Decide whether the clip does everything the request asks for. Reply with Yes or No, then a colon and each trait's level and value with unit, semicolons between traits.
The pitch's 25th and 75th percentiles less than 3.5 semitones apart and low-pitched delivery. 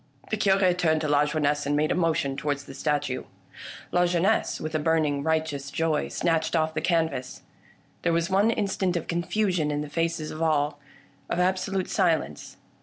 No: average, 3.1 semitones; medium, 160 Hz